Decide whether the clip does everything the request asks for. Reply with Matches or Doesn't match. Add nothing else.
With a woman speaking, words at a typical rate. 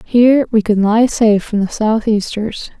Matches